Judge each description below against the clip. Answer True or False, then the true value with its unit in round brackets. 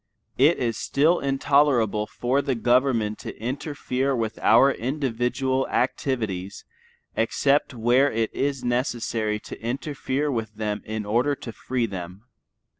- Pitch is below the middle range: True (125 Hz)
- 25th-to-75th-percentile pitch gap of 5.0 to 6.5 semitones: False (3.7 semitones)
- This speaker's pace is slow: True (125 wpm)